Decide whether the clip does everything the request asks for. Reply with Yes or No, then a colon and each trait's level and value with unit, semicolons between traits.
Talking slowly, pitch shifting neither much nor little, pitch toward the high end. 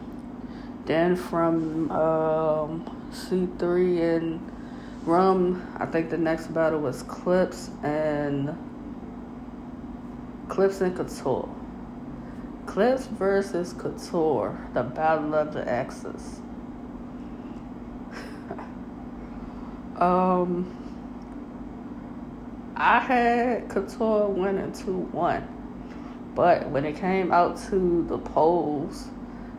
No: slow, 80 wpm; wide, 6.5 semitones; high, 240 Hz